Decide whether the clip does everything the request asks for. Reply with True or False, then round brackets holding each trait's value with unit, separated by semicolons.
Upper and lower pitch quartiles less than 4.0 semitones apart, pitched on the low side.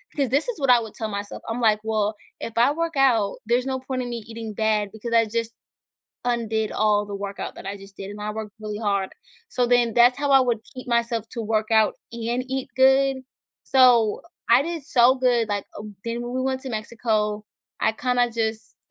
False (2.8 semitones; 230 Hz)